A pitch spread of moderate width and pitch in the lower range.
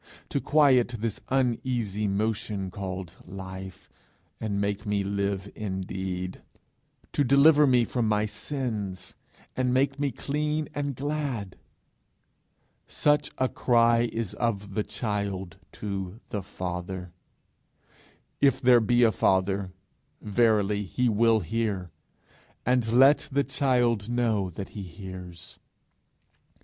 Yes: average, 4.5 semitones; low, 110 Hz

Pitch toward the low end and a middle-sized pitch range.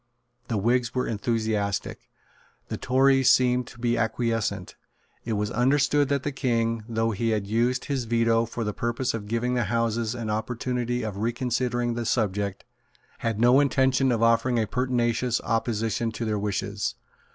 No: low, 115 Hz; narrow, 2.0 semitones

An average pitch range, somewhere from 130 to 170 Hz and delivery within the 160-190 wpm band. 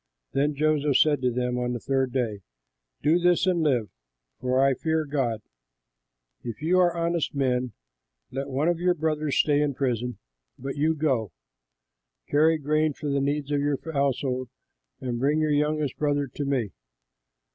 Yes: average, 3.2 semitones; medium, 140 Hz; average, 165 wpm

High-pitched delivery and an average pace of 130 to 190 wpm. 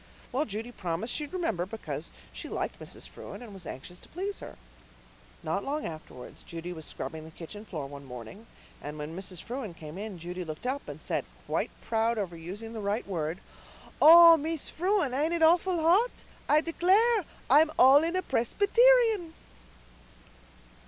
Yes: high, 225 Hz; average, 170 wpm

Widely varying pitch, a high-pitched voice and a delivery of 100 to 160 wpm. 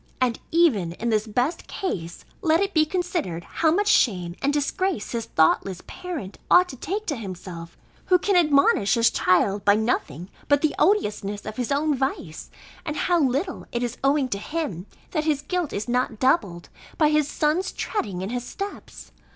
No: wide, 8.1 semitones; very high, 265 Hz; average, 180 wpm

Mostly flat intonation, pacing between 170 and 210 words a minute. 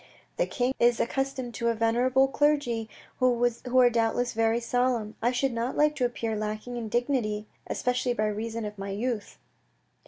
Yes: narrow, 2.1 semitones; average, 175 wpm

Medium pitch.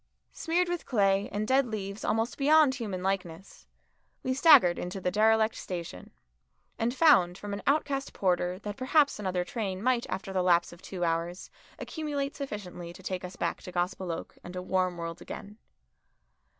No: high, 195 Hz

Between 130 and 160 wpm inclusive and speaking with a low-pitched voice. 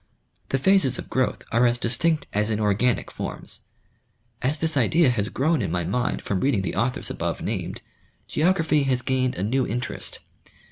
No: average, 175 wpm; low, 125 Hz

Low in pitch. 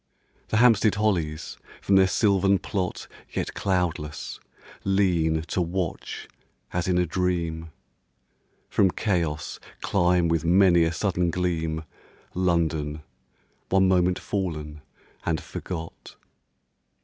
Yes: very low, 90 Hz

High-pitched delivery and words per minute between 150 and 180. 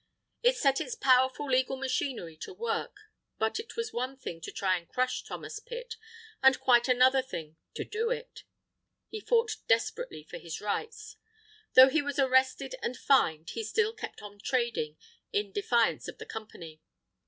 Yes: very high, 260 Hz; average, 165 wpm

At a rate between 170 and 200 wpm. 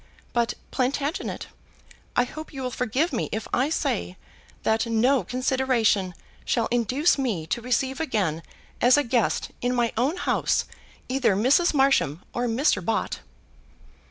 No: average, 140 wpm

